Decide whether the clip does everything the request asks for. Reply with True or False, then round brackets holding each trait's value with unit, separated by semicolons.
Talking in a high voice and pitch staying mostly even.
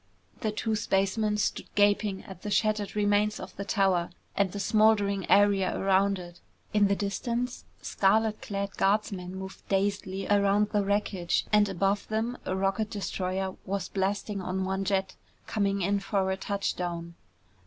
True (200 Hz; 1.5 semitones)